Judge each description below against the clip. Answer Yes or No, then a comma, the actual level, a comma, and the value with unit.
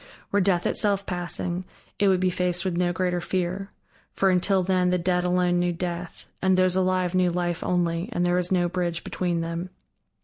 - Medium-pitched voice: Yes, medium, 180 Hz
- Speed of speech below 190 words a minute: No, average, 195 wpm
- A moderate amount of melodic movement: No, narrow, 0.9 semitones